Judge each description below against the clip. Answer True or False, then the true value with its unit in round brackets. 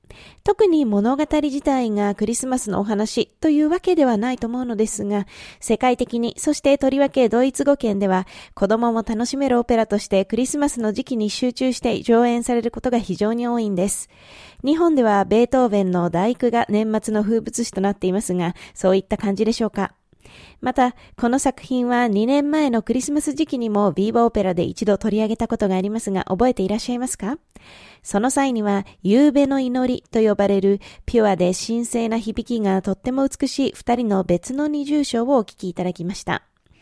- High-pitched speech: True (230 Hz)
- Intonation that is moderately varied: True (4.0 semitones)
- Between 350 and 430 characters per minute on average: True (385 characters per minute)